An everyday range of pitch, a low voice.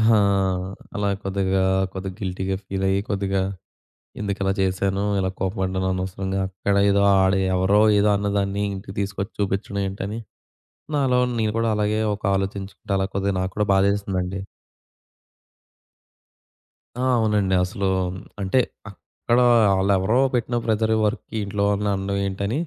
No: narrow, 1.2 semitones; low, 100 Hz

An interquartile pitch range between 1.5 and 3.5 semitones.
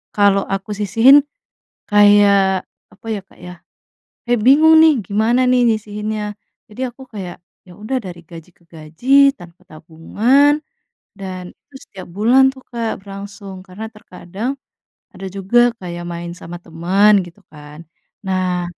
No: average, 4.3 semitones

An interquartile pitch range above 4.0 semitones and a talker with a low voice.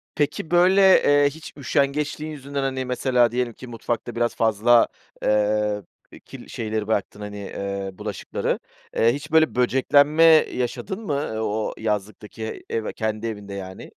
Yes: average, 5.1 semitones; low, 120 Hz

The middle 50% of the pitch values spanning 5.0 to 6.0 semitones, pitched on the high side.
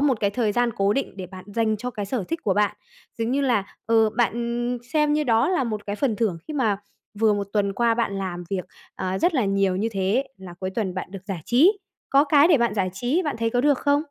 No: average, 4.6 semitones; high, 220 Hz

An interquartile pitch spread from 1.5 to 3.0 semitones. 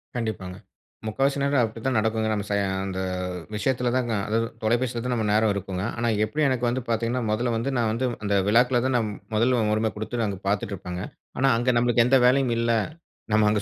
Yes: narrow, 2.6 semitones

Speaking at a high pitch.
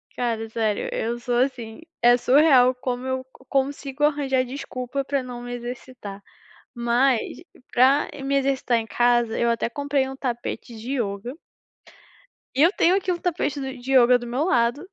Yes: very high, 255 Hz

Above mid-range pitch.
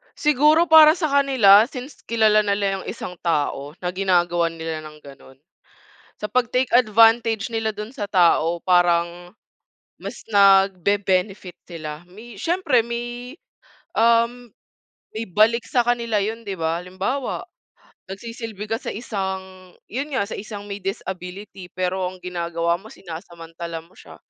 Yes: high, 200 Hz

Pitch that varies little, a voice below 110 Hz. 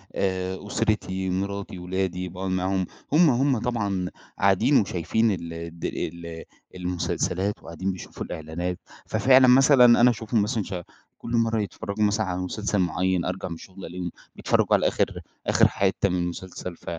No: average, 3.1 semitones; very low, 95 Hz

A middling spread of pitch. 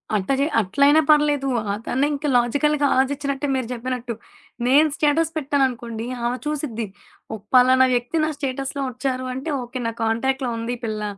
Yes: average, 3.0 semitones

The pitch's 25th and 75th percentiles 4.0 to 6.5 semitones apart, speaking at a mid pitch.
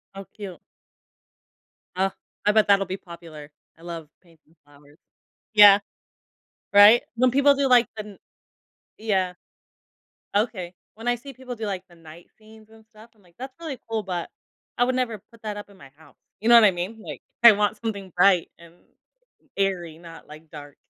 No: average, 4.5 semitones; high, 200 Hz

